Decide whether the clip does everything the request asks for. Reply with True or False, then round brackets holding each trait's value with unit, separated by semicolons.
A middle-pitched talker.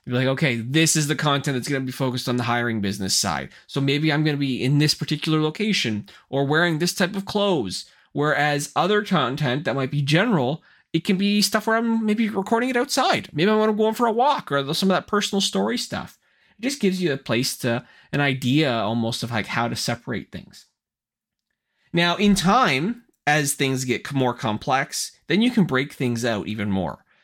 True (150 Hz)